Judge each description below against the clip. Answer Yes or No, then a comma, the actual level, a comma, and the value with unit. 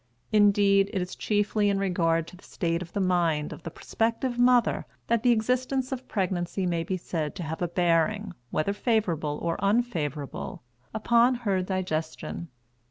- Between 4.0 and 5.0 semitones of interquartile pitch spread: Yes, average, 4.6 semitones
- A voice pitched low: No, high, 190 Hz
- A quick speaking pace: No, average, 165 wpm